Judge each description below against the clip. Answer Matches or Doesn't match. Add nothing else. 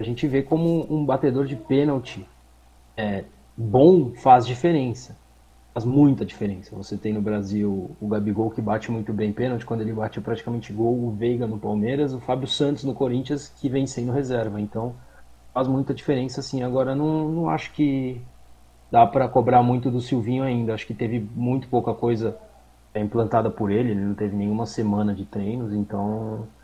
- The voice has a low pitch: Matches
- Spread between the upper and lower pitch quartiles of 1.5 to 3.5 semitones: Doesn't match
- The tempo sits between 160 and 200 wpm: Matches